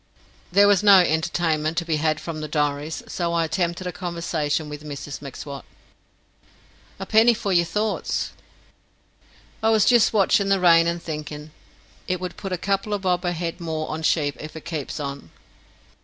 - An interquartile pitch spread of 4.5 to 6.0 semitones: No, average, 3.4 semitones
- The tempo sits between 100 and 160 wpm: No, average, 175 wpm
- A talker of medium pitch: Yes, medium, 170 Hz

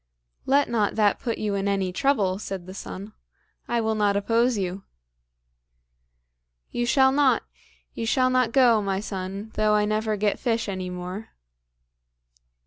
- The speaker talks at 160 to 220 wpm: No, average, 150 wpm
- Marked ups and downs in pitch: No, average, 3.2 semitones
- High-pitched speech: Yes, high, 215 Hz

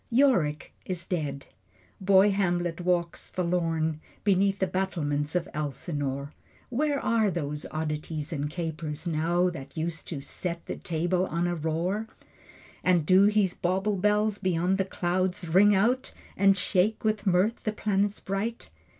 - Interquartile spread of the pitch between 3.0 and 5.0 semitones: Yes, average, 3.6 semitones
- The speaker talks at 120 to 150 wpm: Yes, average, 140 wpm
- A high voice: No, medium, 180 Hz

